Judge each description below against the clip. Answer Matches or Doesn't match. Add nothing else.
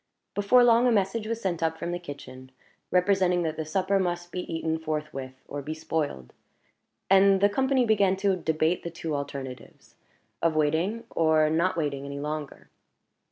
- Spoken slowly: Doesn't match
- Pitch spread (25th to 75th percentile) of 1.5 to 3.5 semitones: Doesn't match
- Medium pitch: Matches